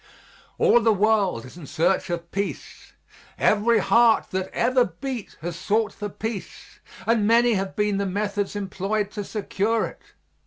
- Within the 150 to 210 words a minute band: Yes, average, 155 wpm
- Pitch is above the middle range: Yes, high, 205 Hz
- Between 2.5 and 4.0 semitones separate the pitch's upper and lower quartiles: Yes, average, 2.8 semitones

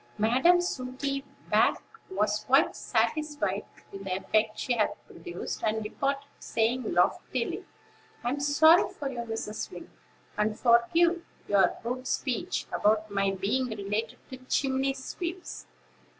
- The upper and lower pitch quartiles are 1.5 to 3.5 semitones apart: No, average, 4.5 semitones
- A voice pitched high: Yes, high, 240 Hz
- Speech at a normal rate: No, slow, 125 wpm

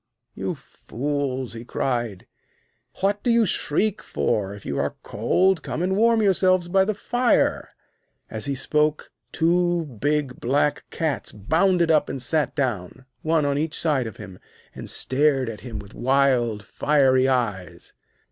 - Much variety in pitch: Yes, wide, 6.3 semitones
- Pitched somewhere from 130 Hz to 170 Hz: Yes, medium, 140 Hz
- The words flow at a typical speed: Yes, average, 150 wpm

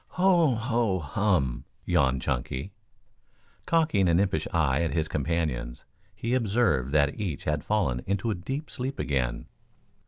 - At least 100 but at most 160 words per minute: Yes, slow, 135 wpm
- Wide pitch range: Yes, wide, 8.4 semitones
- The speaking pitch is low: Yes, very low, 85 Hz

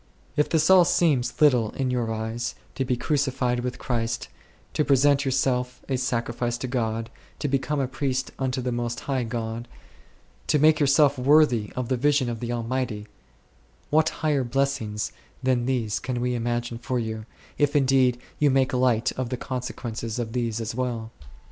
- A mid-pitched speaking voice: No, low, 125 Hz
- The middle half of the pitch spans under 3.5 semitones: Yes, narrow, 2.4 semitones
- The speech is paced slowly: No, average, 175 wpm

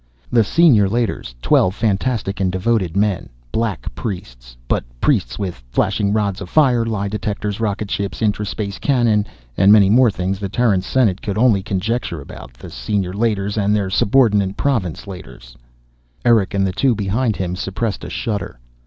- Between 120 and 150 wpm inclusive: No, average, 160 wpm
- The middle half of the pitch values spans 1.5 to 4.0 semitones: Yes, average, 2.9 semitones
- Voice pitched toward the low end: Yes, low, 100 Hz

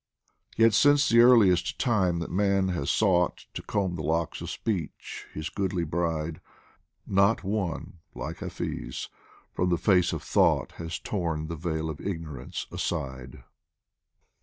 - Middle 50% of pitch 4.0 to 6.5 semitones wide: No, average, 3.5 semitones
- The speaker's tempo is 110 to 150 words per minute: Yes, average, 140 wpm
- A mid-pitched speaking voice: No, very low, 90 Hz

